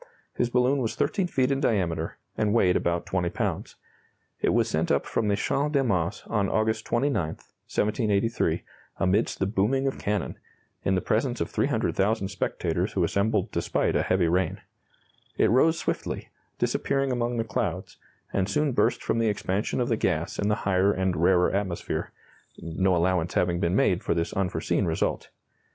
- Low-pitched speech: Yes, low, 100 Hz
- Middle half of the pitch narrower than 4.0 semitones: No, average, 4.3 semitones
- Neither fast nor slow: Yes, average, 170 wpm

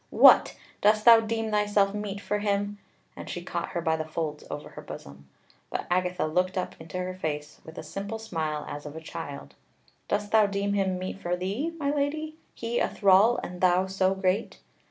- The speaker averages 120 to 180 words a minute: No, average, 195 wpm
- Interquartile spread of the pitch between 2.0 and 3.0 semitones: No, average, 4.2 semitones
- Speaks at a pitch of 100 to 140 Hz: No, high, 190 Hz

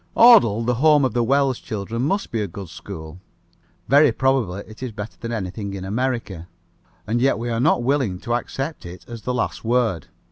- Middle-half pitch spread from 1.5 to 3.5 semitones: No, average, 4.6 semitones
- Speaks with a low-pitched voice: Yes, low, 115 Hz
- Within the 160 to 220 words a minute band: Yes, average, 200 wpm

